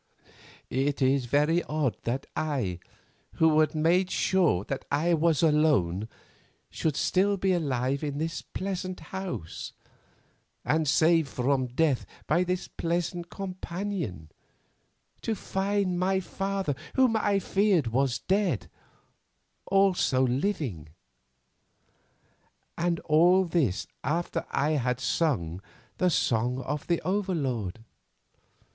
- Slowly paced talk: Yes, slow, 110 wpm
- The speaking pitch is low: No, medium, 155 Hz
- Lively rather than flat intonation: Yes, wide, 5.8 semitones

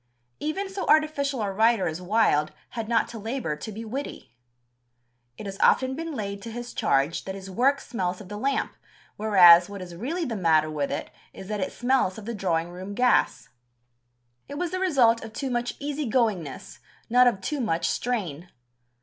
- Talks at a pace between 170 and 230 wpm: Yes, average, 190 wpm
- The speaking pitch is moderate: No, high, 220 Hz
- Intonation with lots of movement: Yes, wide, 6.0 semitones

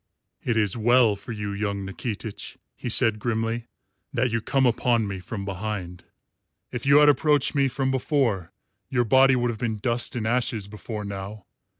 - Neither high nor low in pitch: No, low, 115 Hz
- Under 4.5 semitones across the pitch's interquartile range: Yes, average, 3.5 semitones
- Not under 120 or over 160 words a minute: No, average, 175 wpm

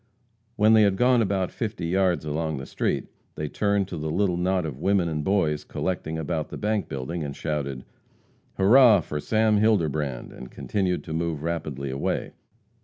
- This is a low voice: Yes, very low, 85 Hz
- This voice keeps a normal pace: Yes, average, 175 wpm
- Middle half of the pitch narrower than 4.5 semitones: No, average, 5.0 semitones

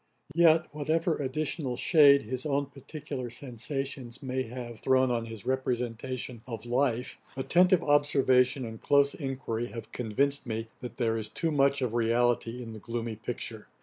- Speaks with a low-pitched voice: Yes, low, 130 Hz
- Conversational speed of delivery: Yes, average, 150 wpm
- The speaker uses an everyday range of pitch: Yes, average, 3.3 semitones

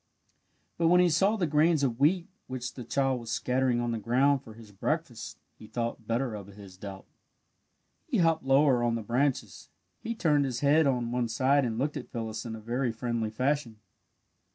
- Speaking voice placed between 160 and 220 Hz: No, low, 125 Hz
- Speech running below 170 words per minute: No, average, 200 wpm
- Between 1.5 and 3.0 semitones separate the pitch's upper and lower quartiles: No, average, 4.0 semitones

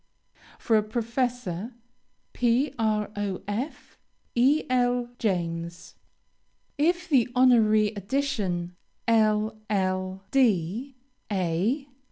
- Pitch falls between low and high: No, high, 220 Hz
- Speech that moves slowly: Yes, slow, 65 wpm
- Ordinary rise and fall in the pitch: Yes, average, 4.4 semitones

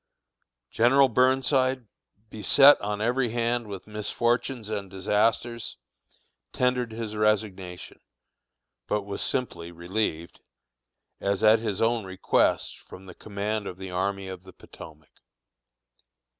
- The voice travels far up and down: No, average, 3.7 semitones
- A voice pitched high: No, low, 105 Hz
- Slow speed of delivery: Yes, slow, 115 wpm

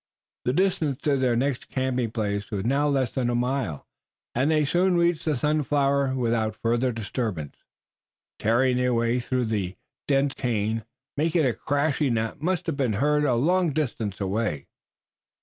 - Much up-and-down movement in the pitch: No, average, 4.2 semitones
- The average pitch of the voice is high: No, low, 130 Hz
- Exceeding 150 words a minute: Yes, average, 160 wpm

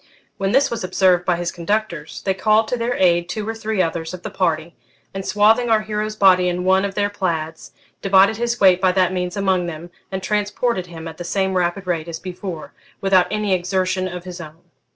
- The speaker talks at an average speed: No, fast, 215 wpm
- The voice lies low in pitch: No, medium, 185 Hz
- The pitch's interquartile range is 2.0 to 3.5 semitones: Yes, average, 2.9 semitones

